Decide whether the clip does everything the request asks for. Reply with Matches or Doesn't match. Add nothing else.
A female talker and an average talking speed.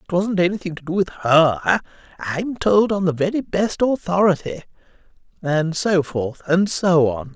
Doesn't match